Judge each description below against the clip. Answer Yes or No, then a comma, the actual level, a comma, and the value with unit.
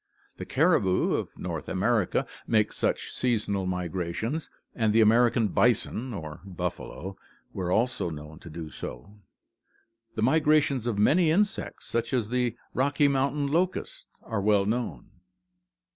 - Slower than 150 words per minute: Yes, average, 140 wpm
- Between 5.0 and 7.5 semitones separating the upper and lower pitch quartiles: Yes, wide, 5.5 semitones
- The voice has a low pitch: Yes, low, 110 Hz